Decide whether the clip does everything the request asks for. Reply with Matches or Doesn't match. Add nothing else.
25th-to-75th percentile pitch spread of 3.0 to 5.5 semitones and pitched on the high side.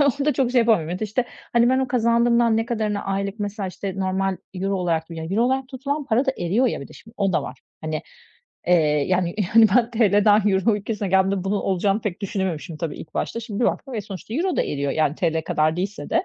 Matches